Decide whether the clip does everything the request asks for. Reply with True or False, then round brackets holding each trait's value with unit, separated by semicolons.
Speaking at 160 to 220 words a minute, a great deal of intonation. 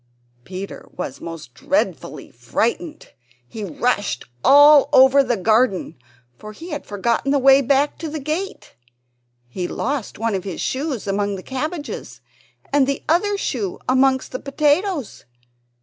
False (140 wpm; 6.2 semitones)